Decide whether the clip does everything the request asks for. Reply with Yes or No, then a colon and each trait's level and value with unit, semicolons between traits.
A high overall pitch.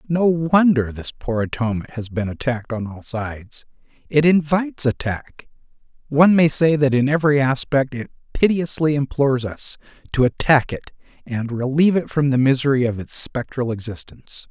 No: low, 135 Hz